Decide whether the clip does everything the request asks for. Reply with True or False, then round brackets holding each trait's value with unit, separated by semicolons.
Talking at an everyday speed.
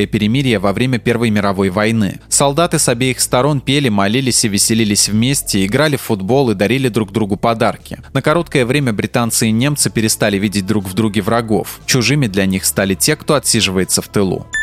False (180 wpm)